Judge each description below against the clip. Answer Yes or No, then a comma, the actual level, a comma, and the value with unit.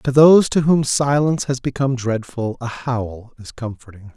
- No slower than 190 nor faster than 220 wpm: No, average, 175 wpm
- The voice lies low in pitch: Yes, low, 125 Hz